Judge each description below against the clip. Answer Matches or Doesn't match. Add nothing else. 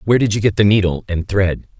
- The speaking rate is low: Doesn't match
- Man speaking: Matches